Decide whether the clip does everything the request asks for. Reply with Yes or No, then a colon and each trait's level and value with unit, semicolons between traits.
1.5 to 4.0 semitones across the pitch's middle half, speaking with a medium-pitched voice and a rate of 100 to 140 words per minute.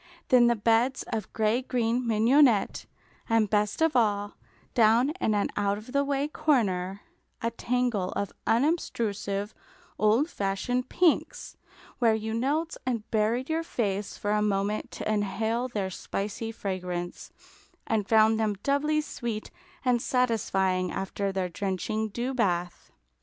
No: average, 3.7 semitones; high, 220 Hz; slow, 135 wpm